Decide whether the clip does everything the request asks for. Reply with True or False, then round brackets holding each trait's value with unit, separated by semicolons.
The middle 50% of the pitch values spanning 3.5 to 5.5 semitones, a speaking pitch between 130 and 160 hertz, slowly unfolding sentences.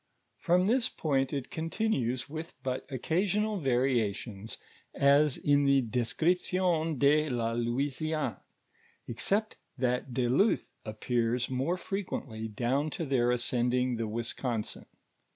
True (4.9 semitones; 135 Hz; 115 wpm)